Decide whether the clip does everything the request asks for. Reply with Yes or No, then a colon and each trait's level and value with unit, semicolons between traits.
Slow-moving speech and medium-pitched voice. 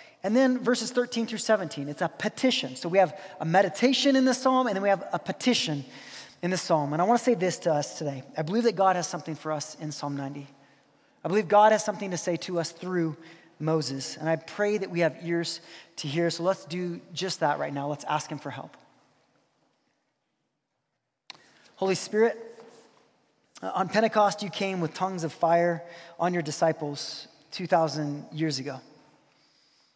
No: average, 190 wpm; medium, 175 Hz